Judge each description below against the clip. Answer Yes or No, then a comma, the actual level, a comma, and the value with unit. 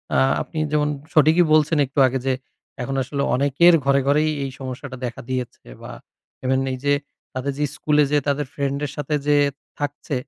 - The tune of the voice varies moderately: No, narrow, 1.9 semitones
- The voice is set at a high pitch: No, medium, 140 Hz